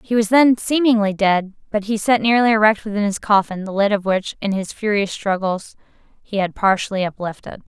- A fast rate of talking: No, average, 195 wpm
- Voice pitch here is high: Yes, high, 205 Hz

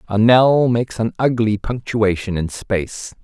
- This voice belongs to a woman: No, male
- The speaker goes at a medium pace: Yes, average, 150 wpm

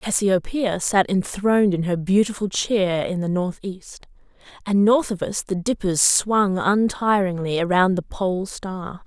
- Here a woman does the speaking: Yes, female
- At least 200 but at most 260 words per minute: No, average, 145 wpm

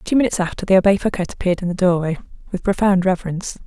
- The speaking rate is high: Yes, fast, 215 wpm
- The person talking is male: No, female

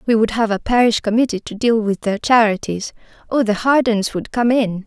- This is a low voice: No, high, 225 Hz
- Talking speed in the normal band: Yes, average, 195 wpm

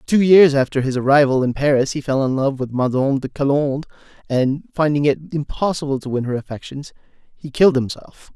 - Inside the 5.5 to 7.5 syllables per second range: Yes, 5.9 syllables/s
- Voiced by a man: Yes, male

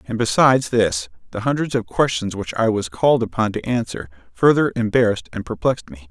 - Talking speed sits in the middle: Yes, average, 185 wpm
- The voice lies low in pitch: Yes, low, 110 Hz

